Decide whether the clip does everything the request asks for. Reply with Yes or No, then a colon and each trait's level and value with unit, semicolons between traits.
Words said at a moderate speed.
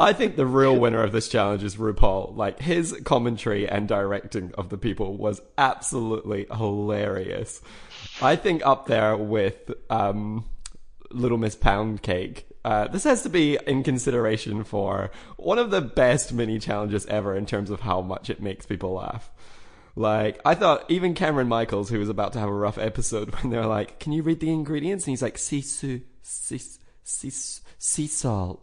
Yes: average, 180 wpm